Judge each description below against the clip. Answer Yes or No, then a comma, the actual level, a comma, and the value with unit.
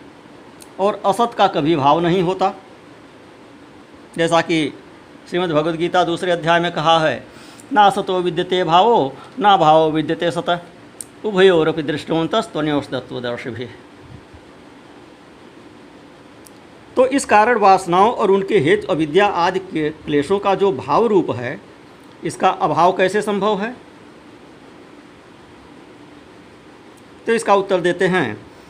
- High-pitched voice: No, medium, 175 Hz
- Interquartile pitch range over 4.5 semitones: No, average, 3.7 semitones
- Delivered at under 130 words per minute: Yes, average, 115 wpm